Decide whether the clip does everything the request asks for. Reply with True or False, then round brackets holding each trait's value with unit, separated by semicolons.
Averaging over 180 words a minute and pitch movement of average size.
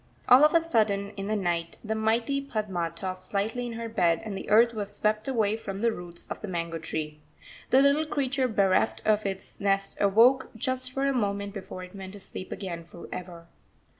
True (205 wpm; 4.0 semitones)